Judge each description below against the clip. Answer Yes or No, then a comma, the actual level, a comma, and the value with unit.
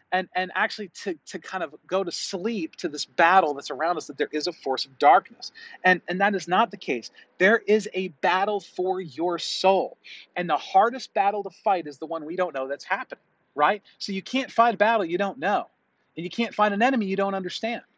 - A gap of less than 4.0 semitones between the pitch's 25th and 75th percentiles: Yes, average, 3.3 semitones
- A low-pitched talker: No, high, 195 Hz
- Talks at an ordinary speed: No, fast, 235 wpm